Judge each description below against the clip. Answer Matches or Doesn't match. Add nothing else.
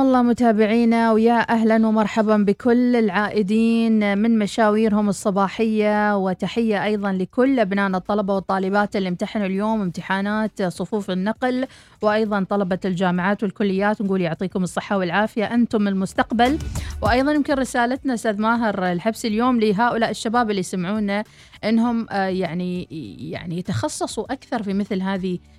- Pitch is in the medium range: Doesn't match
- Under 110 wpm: Doesn't match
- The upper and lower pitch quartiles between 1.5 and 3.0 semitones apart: Matches